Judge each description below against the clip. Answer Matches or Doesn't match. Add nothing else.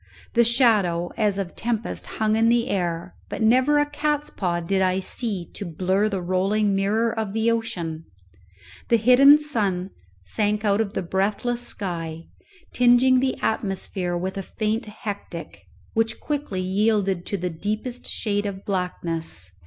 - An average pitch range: Matches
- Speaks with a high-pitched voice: Matches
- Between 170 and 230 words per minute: Doesn't match